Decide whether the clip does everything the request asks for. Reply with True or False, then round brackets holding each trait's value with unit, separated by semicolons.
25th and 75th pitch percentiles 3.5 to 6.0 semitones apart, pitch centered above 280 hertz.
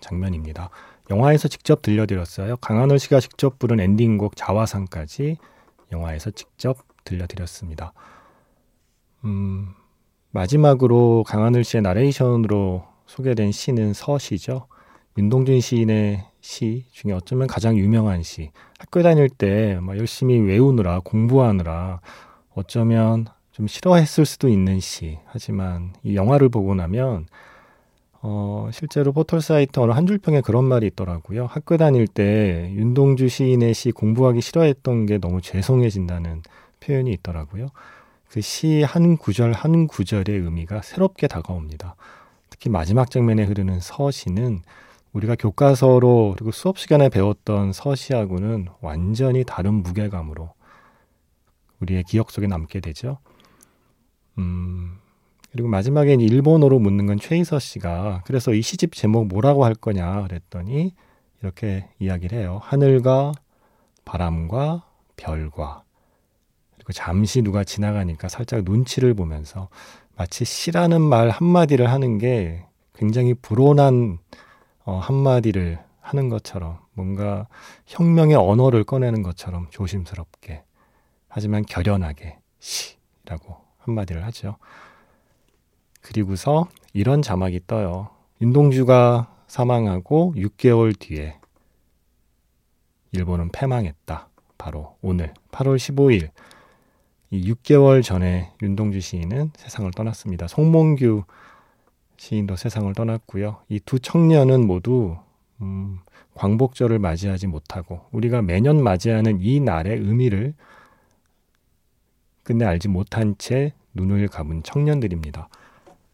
False (5.6 semitones; 110 Hz)